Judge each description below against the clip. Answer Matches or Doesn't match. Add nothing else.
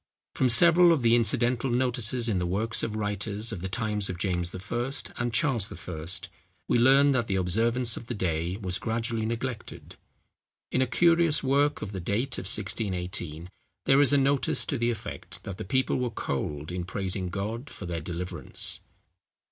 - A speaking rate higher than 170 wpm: Matches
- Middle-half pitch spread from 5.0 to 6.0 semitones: Matches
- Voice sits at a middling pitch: Doesn't match